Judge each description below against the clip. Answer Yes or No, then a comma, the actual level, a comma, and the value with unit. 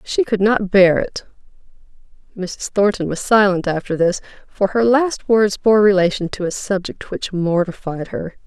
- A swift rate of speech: No, average, 165 wpm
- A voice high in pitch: Yes, high, 195 Hz